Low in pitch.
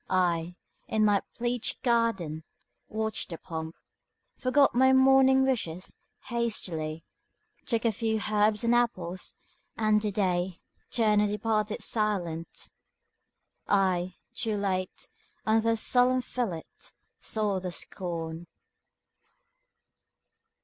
No: high, 210 Hz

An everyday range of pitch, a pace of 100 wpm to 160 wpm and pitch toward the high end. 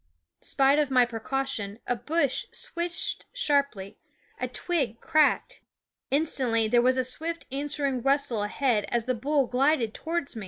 Yes: average, 3.7 semitones; average, 145 wpm; very high, 270 Hz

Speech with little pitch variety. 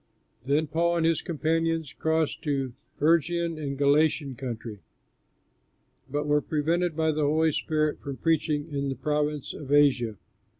Yes: narrow, 2.3 semitones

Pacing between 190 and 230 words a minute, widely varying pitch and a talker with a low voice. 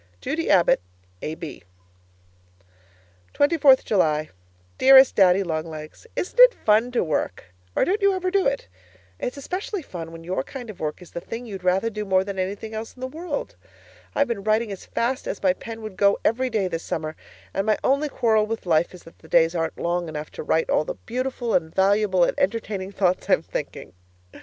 No: average, 195 wpm; wide, 6.5 semitones; high, 200 Hz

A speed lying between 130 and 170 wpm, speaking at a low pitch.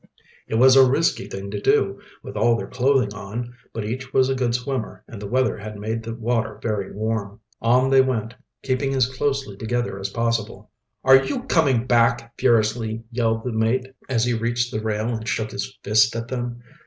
No: average, 195 wpm; low, 115 Hz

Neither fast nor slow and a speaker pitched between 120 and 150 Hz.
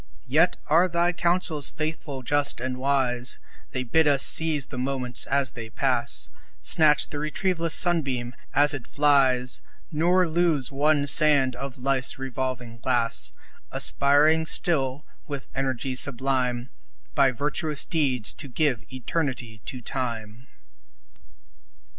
No: slow, 125 wpm; low, 135 Hz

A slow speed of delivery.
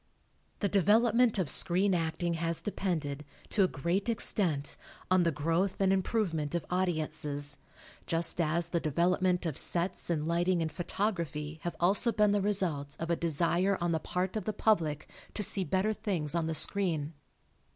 No: average, 170 wpm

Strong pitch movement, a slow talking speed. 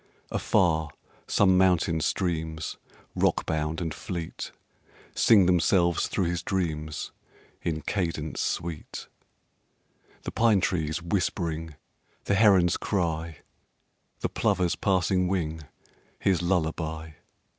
No: average, 2.7 semitones; slow, 95 wpm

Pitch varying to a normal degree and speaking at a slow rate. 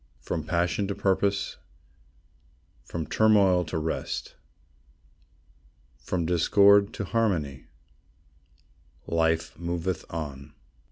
Yes: average, 3.6 semitones; slow, 80 wpm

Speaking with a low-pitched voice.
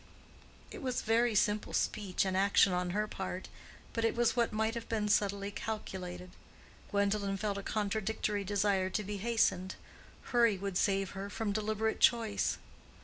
No: high, 205 Hz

